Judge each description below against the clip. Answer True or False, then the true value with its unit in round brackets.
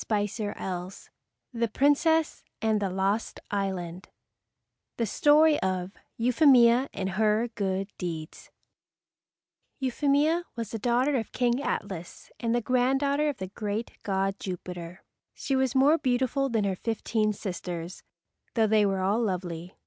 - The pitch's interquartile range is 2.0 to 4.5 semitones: False (5.1 semitones)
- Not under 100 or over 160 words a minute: True (135 wpm)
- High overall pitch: True (220 Hz)